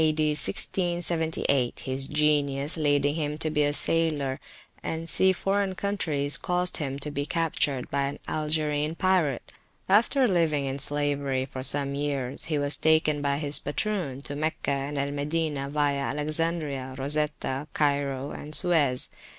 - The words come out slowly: No, average, 150 wpm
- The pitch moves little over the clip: Yes, narrow, 2.3 semitones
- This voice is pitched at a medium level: Yes, medium, 145 Hz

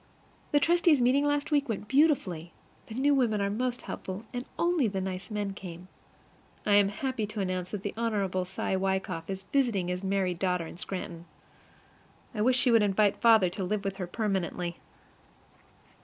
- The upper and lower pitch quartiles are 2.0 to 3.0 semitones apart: No, average, 4.7 semitones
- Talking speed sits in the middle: Yes, average, 175 wpm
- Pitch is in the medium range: No, high, 205 Hz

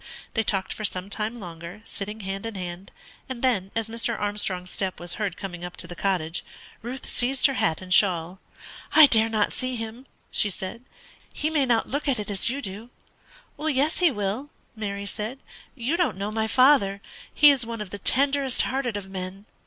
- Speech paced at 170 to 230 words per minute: Yes, average, 195 wpm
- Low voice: No, high, 215 Hz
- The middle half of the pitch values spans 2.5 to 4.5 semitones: No, average, 4.9 semitones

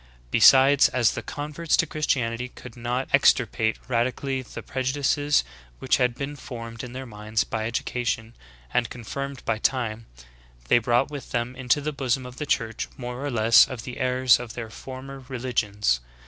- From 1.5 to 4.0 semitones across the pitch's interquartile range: Yes, narrow, 2.5 semitones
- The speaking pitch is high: No, low, 125 Hz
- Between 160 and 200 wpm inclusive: Yes, average, 170 wpm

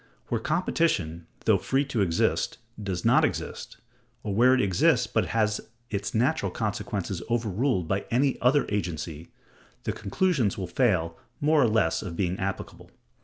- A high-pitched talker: No, low, 105 Hz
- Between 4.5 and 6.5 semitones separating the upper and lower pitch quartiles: Yes, wide, 5.5 semitones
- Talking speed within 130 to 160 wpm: Yes, average, 150 wpm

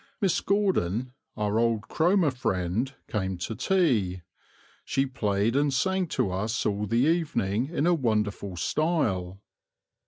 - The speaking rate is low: Yes, slow, 130 wpm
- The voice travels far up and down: Yes, wide, 7.7 semitones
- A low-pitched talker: Yes, low, 115 Hz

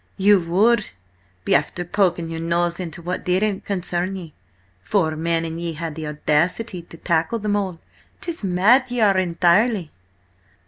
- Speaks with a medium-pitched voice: Yes, medium, 180 Hz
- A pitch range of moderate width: Yes, average, 3.4 semitones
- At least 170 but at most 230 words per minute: No, average, 155 wpm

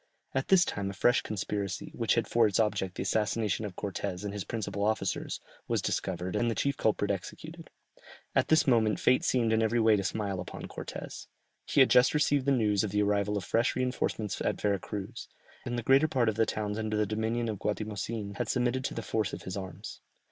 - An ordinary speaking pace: No, fast, 215 wpm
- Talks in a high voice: No, low, 110 Hz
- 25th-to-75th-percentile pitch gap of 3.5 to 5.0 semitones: No, average, 2.7 semitones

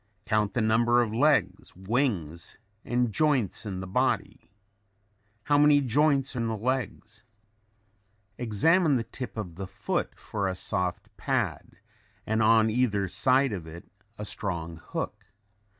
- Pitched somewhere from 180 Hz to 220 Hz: No, low, 110 Hz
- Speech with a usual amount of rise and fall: Yes, average, 4.7 semitones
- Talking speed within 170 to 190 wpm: No, slow, 135 wpm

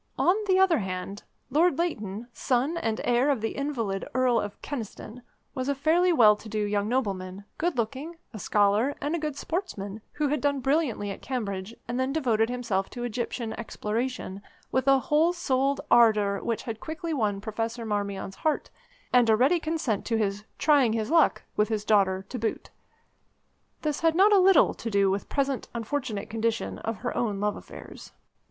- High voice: Yes, high, 235 Hz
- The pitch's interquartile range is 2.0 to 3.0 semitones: No, wide, 5.4 semitones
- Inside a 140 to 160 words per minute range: No, average, 185 wpm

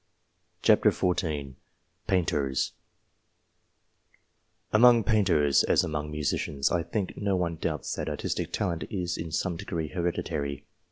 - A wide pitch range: No, average, 3.8 semitones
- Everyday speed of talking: No, slow, 115 wpm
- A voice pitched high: No, very low, 85 Hz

